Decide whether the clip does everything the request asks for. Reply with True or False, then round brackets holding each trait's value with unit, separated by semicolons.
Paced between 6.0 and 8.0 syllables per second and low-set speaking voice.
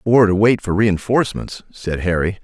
False (4.9 syllables/s; 100 Hz)